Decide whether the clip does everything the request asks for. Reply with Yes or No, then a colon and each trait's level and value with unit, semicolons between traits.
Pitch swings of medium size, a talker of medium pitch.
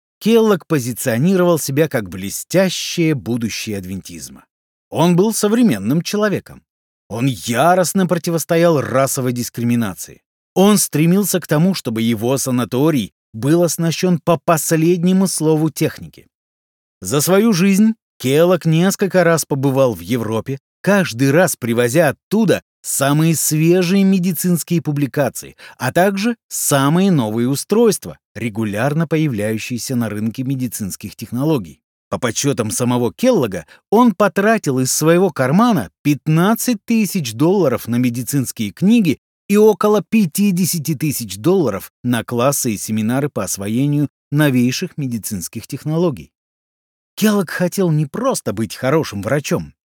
No: wide, 7.2 semitones; medium, 150 Hz